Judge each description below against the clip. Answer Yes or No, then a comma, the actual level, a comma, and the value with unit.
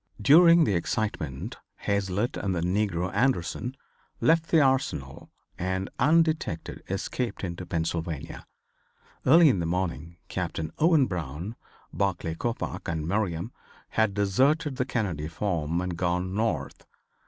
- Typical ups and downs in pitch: No, wide, 6.5 semitones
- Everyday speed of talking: No, slow, 120 wpm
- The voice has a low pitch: Yes, very low, 95 Hz